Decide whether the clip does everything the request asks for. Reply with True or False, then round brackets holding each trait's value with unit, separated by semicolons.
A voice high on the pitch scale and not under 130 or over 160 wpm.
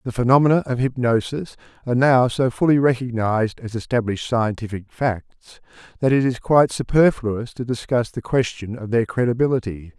False (120 Hz; 150 wpm)